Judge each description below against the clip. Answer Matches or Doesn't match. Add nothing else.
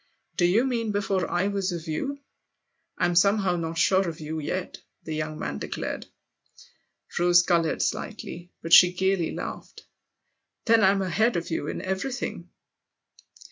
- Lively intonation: Doesn't match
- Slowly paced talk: Doesn't match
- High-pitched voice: Doesn't match